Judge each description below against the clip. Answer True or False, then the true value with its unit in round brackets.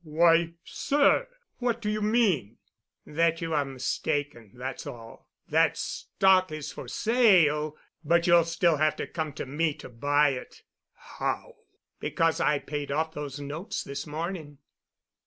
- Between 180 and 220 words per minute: False (140 wpm)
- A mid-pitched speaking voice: True (155 Hz)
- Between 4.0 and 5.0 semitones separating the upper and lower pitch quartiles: False (3.2 semitones)